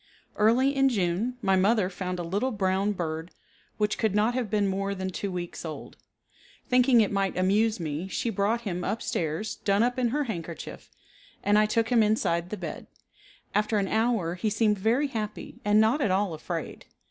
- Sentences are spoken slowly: No, average, 190 wpm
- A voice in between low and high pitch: No, high, 205 Hz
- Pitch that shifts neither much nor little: Yes, average, 3.4 semitones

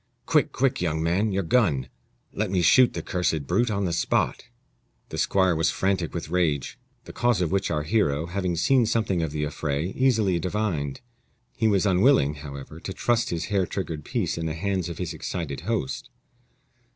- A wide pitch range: No, average, 4.7 semitones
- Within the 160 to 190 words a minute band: Yes, average, 185 wpm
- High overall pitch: No, very low, 90 Hz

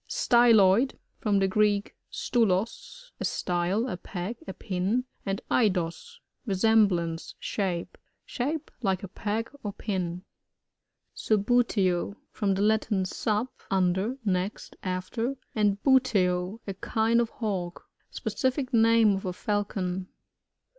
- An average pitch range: Yes, average, 3.6 semitones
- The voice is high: Yes, high, 205 Hz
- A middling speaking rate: No, slow, 125 wpm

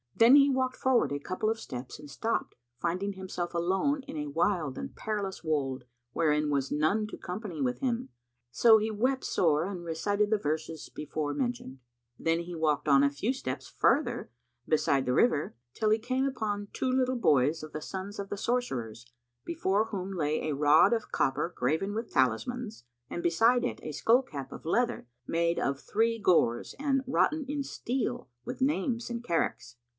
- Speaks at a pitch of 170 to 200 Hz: Yes, high, 190 Hz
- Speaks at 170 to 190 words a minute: Yes, average, 180 wpm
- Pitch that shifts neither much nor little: No, wide, 7.6 semitones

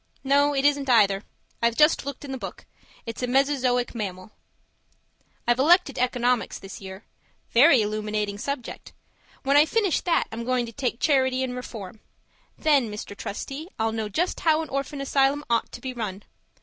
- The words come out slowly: No, average, 170 wpm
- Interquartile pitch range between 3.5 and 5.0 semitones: Yes, average, 4.1 semitones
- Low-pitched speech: No, very high, 250 Hz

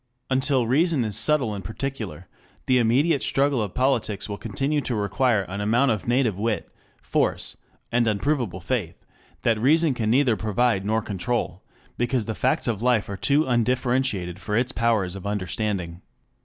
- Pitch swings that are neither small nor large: Yes, average, 4.2 semitones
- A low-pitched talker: Yes, low, 115 Hz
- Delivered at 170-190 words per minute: No, average, 160 wpm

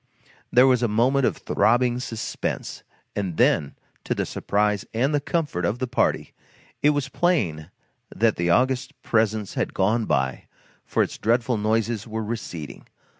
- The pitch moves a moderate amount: Yes, average, 3.5 semitones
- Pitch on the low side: Yes, low, 115 Hz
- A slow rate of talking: No, average, 155 wpm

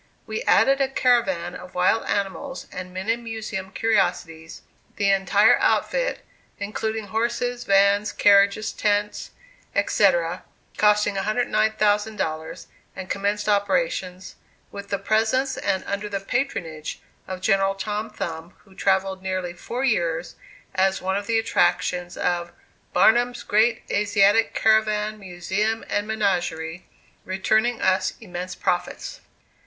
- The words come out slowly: Yes, slow, 115 wpm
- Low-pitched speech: No, high, 200 Hz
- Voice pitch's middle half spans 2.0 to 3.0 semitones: Yes, average, 2.7 semitones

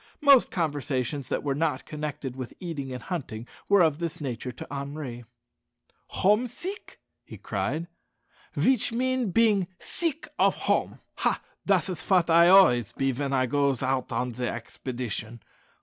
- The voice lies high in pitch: No, medium, 145 Hz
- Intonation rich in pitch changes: Yes, wide, 6.6 semitones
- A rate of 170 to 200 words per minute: No, average, 155 wpm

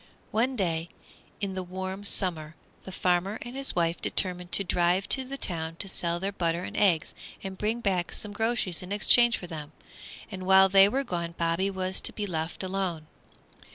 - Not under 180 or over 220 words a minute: Yes, average, 190 wpm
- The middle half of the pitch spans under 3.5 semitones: Yes, average, 2.8 semitones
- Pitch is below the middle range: No, medium, 185 Hz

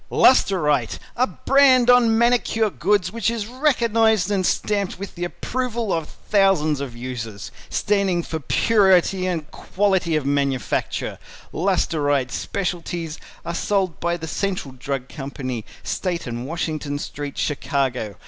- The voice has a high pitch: No, medium, 175 Hz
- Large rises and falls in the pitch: Yes, wide, 6.4 semitones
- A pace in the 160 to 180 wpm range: No, average, 140 wpm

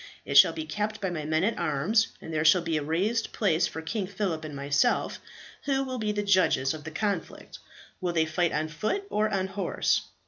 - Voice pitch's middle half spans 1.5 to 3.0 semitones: No, average, 5.1 semitones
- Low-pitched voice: No, medium, 180 Hz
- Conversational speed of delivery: No, fast, 215 wpm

